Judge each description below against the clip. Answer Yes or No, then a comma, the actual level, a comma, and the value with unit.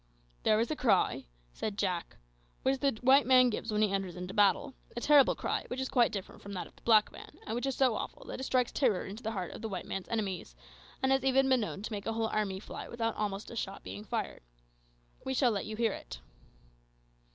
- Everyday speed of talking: No, fast, 240 wpm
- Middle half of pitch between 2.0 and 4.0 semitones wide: No, average, 4.5 semitones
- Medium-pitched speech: No, high, 220 Hz